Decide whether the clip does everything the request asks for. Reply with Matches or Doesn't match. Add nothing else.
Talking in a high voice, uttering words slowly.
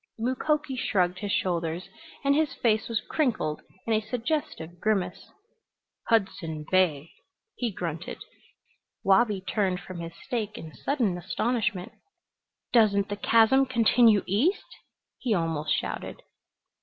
Matches